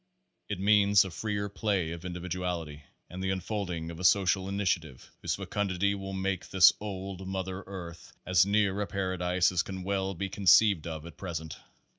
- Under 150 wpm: No, average, 170 wpm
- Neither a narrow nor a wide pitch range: No, narrow, 2.0 semitones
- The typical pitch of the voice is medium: No, very low, 95 Hz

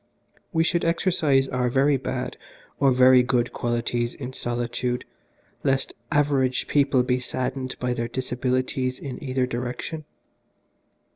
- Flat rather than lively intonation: Yes, narrow, 1.7 semitones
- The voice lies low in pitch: Yes, low, 130 Hz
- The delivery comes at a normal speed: No, slow, 125 wpm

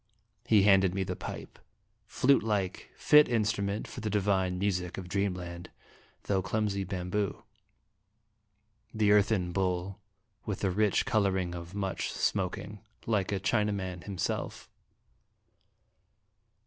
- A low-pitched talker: Yes, low, 100 Hz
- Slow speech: Yes, slow, 120 wpm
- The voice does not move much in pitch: Yes, narrow, 2.3 semitones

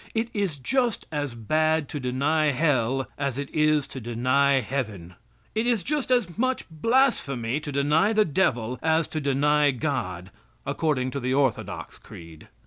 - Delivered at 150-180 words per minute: Yes, average, 155 wpm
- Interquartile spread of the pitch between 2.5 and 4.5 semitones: Yes, average, 4.1 semitones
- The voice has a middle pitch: Yes, medium, 145 Hz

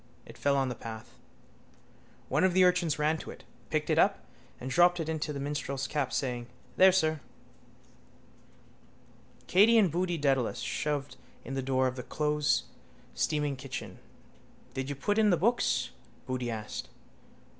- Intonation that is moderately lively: Yes, average, 4.8 semitones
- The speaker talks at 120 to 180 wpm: Yes, average, 155 wpm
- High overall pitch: No, medium, 145 Hz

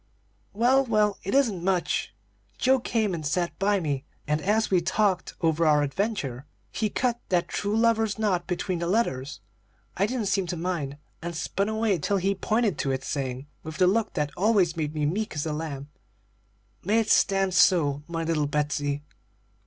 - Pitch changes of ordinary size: No, wide, 5.8 semitones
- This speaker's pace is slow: No, average, 180 wpm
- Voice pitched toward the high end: No, medium, 180 Hz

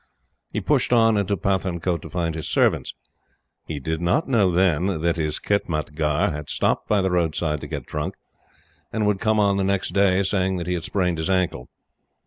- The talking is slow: No, average, 190 wpm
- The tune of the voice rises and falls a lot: No, average, 3.4 semitones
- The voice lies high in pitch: No, very low, 90 Hz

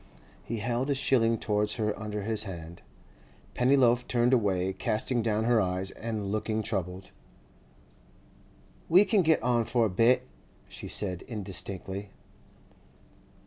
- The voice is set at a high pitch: No, low, 110 Hz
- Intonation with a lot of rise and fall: No, average, 3.6 semitones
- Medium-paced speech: No, slow, 130 wpm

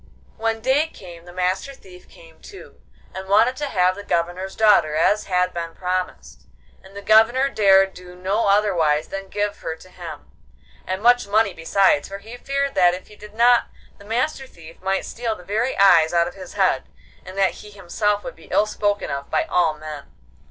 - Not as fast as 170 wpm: No, average, 195 wpm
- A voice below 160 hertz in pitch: No, high, 195 Hz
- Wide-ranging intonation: No, average, 3.5 semitones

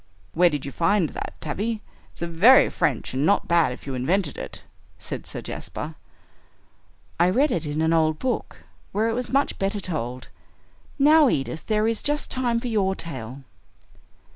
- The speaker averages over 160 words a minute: Yes, average, 170 wpm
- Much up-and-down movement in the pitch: Yes, wide, 7.1 semitones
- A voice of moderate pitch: Yes, medium, 180 Hz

